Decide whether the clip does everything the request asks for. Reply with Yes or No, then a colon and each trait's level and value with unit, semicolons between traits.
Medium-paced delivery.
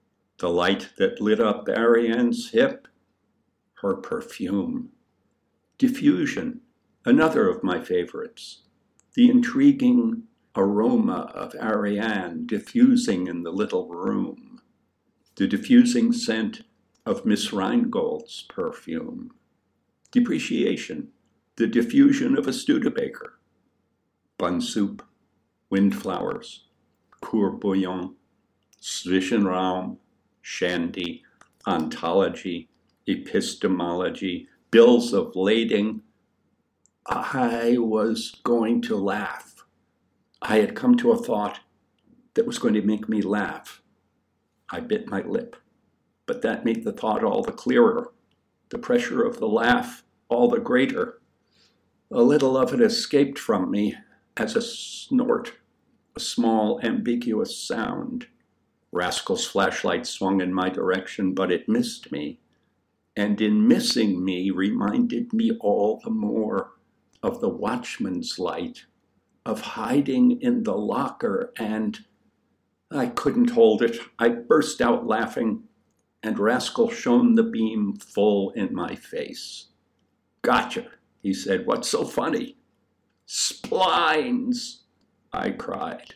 No: slow, 110 wpm